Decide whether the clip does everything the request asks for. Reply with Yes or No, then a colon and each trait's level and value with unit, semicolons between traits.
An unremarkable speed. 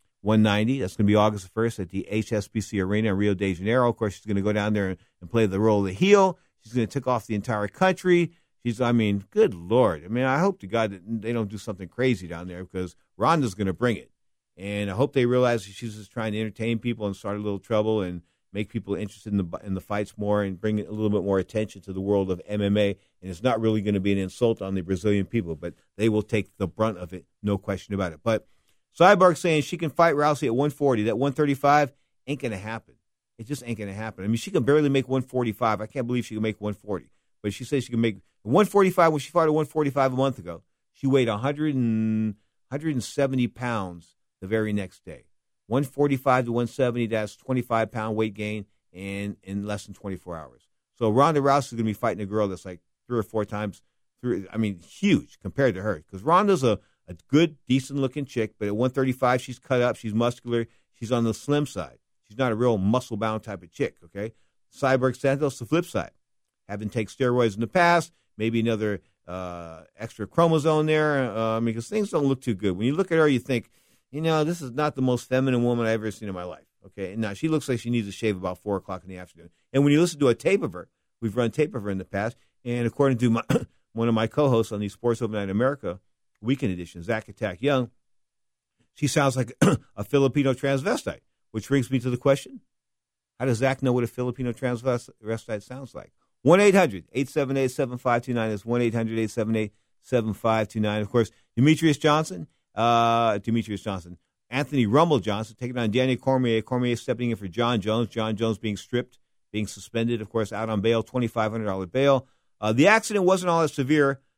No: fast, 230 wpm